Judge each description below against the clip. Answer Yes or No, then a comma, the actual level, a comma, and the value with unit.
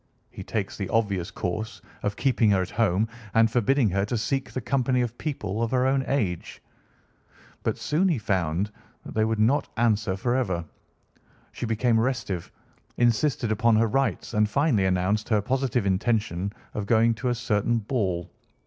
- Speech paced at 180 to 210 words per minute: No, average, 165 wpm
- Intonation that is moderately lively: Yes, average, 3.5 semitones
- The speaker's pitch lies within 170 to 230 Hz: No, low, 110 Hz